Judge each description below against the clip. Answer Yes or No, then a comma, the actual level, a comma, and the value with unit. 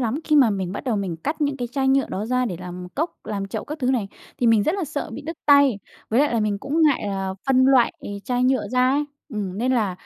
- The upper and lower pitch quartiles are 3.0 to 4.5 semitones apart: No, wide, 5.5 semitones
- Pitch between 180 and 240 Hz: No, very high, 250 Hz